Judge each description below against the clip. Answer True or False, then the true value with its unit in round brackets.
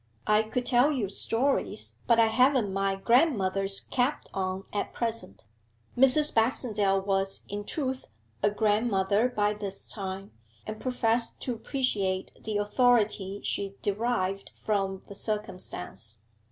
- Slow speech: True (125 wpm)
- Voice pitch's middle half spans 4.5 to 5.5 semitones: False (3.8 semitones)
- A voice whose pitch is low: False (210 Hz)